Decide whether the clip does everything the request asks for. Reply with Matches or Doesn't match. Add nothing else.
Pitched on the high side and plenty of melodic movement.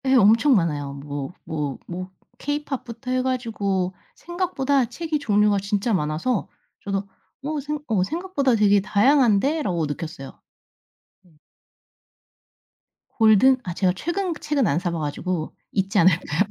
Matches